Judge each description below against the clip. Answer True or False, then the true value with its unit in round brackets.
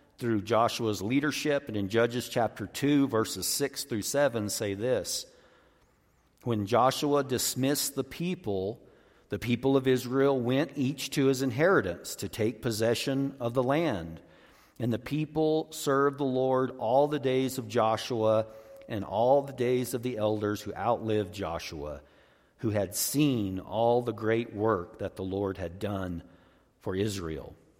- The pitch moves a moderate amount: True (4.8 semitones)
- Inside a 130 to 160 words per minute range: True (150 wpm)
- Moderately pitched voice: False (120 Hz)